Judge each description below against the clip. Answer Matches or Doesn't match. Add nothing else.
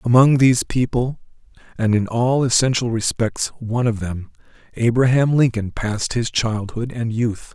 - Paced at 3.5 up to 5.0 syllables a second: Matches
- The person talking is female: Doesn't match